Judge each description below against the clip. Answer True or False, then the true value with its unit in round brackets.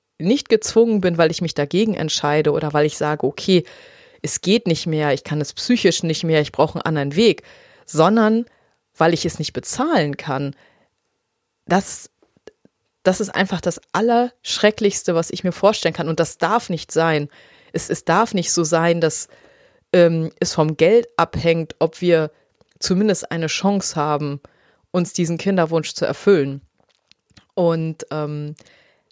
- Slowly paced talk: False (155 wpm)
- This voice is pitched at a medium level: True (170 Hz)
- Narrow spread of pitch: False (4.1 semitones)